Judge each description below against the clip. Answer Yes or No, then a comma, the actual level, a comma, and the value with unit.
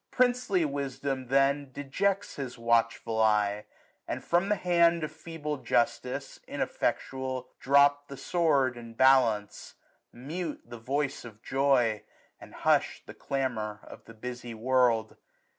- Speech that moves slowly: Yes, slow, 130 wpm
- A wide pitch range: No, average, 3.7 semitones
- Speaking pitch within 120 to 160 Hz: Yes, low, 135 Hz